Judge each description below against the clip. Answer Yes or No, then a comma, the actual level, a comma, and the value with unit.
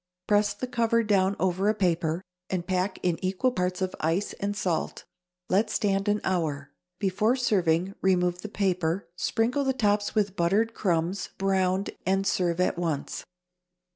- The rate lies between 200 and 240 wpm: No, average, 155 wpm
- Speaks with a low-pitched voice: No, high, 190 Hz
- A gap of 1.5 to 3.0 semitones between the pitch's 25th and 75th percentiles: Yes, narrow, 2.5 semitones